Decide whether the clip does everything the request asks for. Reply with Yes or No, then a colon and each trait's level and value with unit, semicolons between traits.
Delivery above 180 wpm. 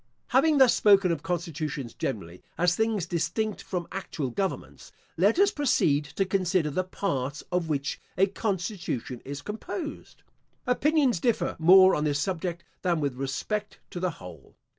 No: average, 155 wpm